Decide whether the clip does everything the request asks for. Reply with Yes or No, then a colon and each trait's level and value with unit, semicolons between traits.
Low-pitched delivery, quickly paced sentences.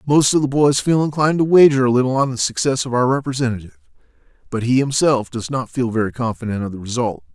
Yes: low, 130 Hz; fast, 220 wpm